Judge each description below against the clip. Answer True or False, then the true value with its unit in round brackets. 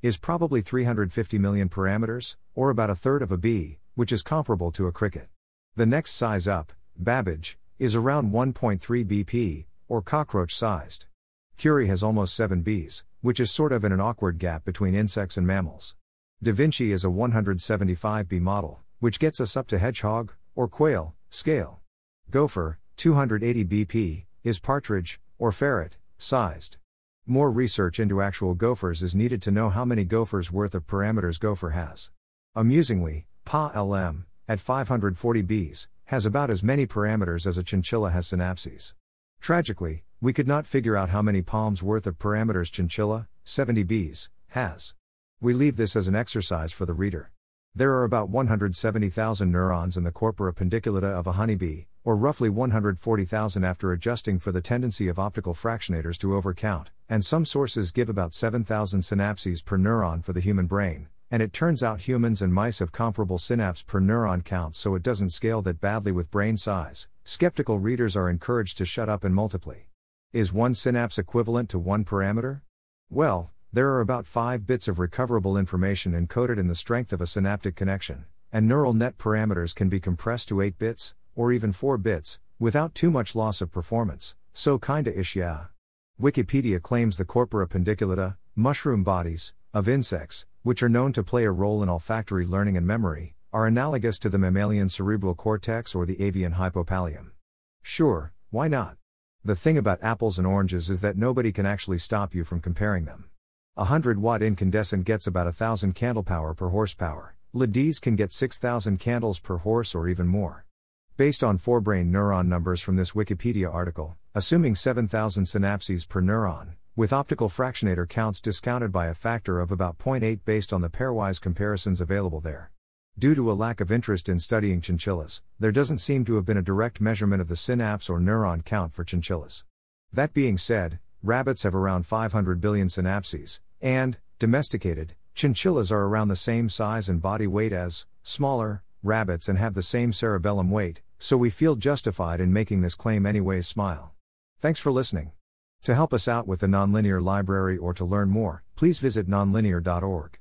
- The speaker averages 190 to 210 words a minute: False (175 wpm)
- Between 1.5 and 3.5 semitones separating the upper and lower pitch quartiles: False (4.2 semitones)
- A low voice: True (100 Hz)